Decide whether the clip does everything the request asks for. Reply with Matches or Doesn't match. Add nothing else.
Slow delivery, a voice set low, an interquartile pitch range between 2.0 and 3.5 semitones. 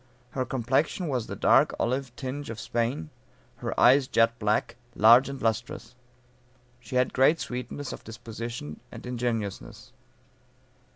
Matches